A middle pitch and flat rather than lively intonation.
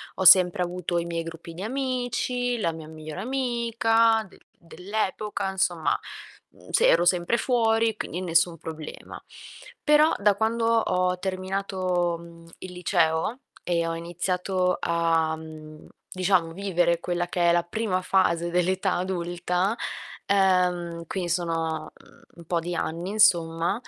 No: medium, 180 Hz; average, 3.0 semitones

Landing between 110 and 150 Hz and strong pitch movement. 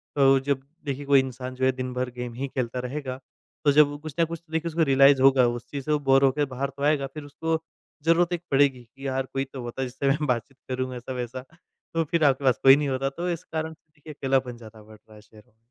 No: low, 135 Hz; narrow, 2.4 semitones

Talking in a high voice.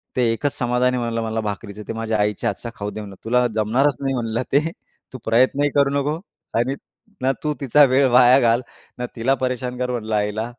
No: low, 120 Hz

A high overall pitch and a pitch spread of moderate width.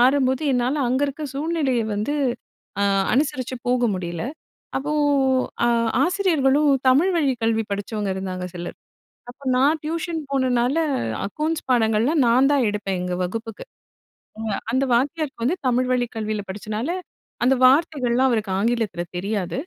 Yes: very high, 250 Hz; average, 4.8 semitones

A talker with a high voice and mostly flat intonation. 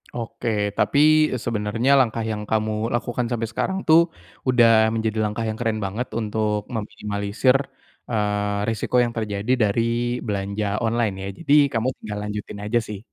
No: low, 110 Hz; narrow, 2.1 semitones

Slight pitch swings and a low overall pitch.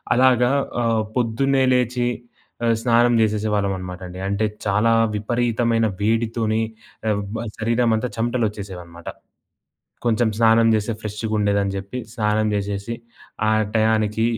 Yes: narrow, 2.2 semitones; low, 110 Hz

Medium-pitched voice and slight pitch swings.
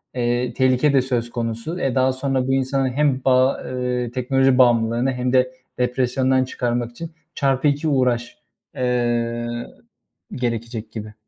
No: low, 125 Hz; narrow, 1.8 semitones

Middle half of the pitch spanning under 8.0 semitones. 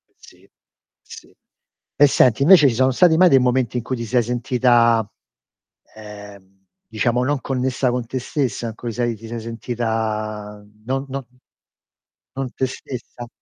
Yes: average, 2.7 semitones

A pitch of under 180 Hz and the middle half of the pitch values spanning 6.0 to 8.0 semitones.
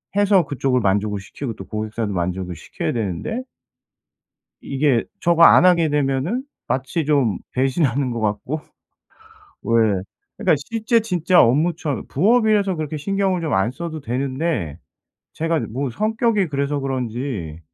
Yes: medium, 140 Hz; wide, 6.8 semitones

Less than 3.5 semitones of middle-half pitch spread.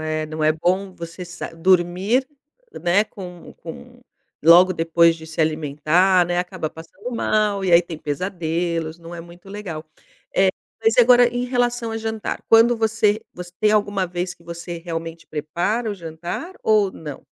No: average, 4.1 semitones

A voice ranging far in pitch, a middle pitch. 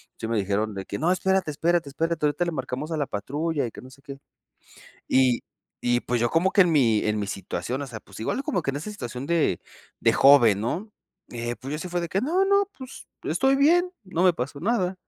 Yes: wide, 7.0 semitones; medium, 145 Hz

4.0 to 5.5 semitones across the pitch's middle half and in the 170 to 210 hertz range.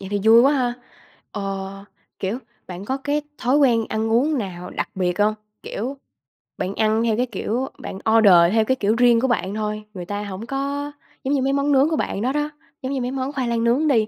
No: average, 4.6 semitones; high, 235 Hz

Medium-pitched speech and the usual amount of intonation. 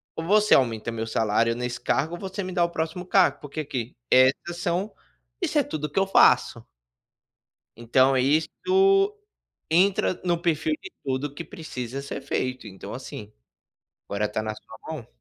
No: medium, 145 Hz; wide, 6.1 semitones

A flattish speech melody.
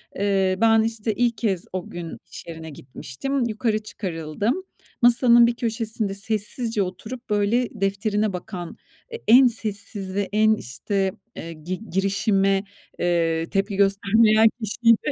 No: average, 3.2 semitones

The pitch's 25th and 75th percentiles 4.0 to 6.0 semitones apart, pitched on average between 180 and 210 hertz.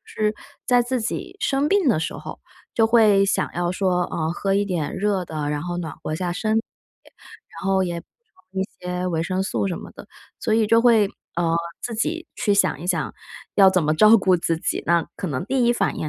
Yes: average, 4.4 semitones; high, 190 Hz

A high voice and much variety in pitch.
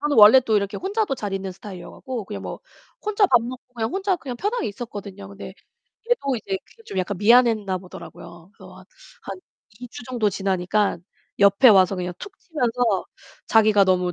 No: high, 215 Hz; average, 4.7 semitones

